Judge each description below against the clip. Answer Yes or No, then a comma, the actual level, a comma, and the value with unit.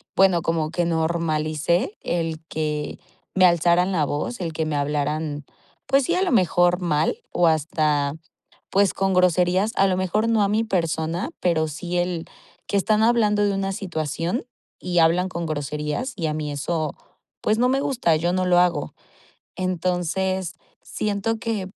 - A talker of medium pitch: Yes, medium, 175 Hz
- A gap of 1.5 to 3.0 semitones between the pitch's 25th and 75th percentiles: No, average, 3.5 semitones